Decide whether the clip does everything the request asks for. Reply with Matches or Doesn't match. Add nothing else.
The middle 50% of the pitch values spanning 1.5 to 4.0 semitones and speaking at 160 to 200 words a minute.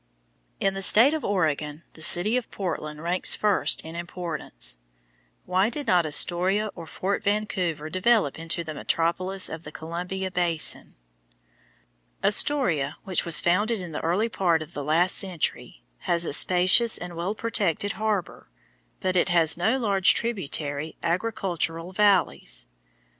Doesn't match